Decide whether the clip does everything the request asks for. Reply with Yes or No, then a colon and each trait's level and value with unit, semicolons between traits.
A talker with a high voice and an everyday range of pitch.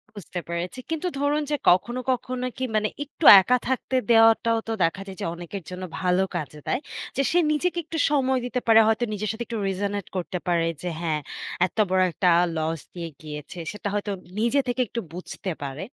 No: high, 205 Hz; wide, 5.9 semitones